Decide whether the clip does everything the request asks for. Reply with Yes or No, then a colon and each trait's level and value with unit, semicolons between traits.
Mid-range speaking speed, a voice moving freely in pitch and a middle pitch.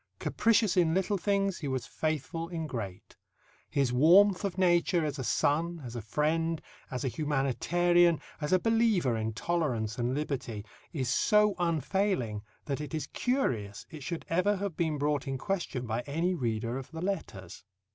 Yes: average, 165 wpm; wide, 5.7 semitones; medium, 155 Hz